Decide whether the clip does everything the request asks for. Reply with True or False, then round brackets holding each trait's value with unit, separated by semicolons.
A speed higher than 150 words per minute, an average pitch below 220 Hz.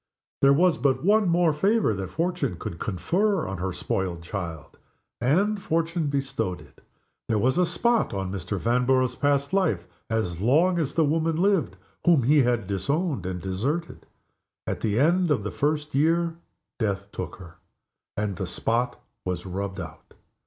True (160 wpm; 135 Hz)